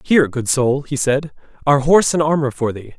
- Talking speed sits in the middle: No, fast, 220 wpm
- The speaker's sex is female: No, male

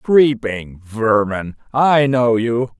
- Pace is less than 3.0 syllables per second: Yes, 2.7 syllables/s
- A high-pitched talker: No, low, 120 Hz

